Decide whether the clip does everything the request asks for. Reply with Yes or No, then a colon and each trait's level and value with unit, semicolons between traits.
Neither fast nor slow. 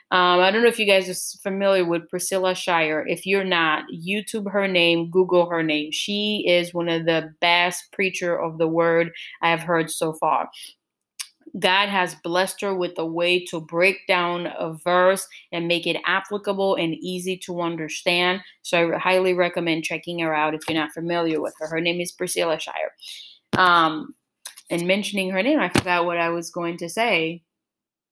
Yes: average, 185 wpm